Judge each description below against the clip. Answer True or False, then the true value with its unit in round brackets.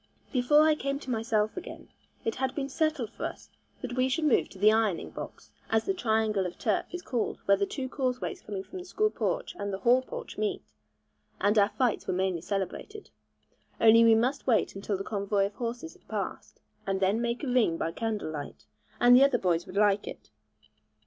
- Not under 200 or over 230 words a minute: True (205 wpm)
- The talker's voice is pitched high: True (230 Hz)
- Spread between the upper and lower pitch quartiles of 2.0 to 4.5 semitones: False (5.0 semitones)